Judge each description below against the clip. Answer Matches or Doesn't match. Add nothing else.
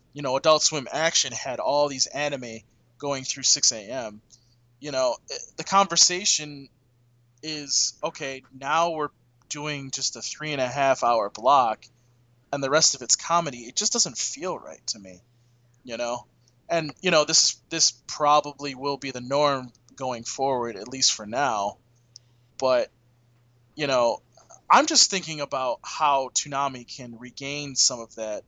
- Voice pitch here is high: Doesn't match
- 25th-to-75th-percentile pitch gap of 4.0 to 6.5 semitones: Doesn't match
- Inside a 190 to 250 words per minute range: Doesn't match